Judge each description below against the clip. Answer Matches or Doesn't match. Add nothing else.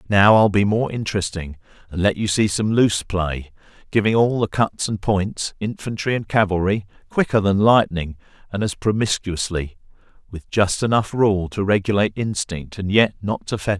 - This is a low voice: Matches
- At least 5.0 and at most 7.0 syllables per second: Matches